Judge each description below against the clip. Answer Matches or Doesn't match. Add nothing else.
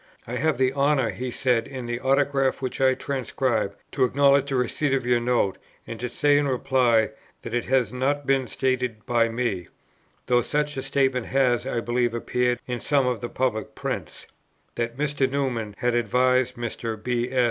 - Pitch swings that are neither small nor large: Doesn't match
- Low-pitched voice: Matches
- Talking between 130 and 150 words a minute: Doesn't match